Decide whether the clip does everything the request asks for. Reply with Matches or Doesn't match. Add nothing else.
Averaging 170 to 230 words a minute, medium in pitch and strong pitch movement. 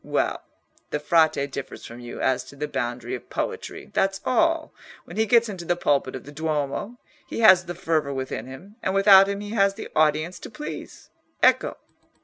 Matches